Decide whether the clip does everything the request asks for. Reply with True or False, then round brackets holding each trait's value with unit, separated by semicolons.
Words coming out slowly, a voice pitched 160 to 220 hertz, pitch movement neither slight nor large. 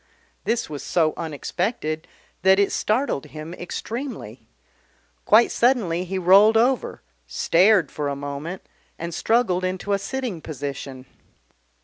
False (120 wpm; 185 Hz; 5.9 semitones)